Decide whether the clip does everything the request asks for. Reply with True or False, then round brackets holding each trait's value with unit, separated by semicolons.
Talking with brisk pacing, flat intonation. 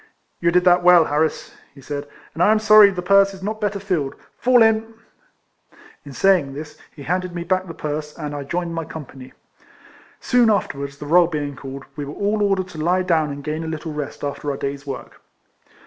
False (210 wpm; 4.7 semitones)